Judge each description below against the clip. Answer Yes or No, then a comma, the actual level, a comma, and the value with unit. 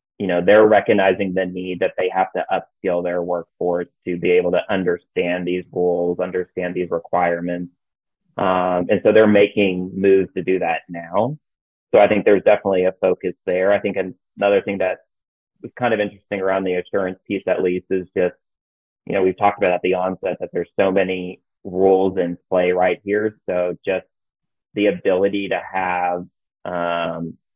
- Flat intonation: Yes, narrow, 1.4 semitones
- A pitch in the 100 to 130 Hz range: No, very low, 90 Hz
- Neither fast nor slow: Yes, average, 180 wpm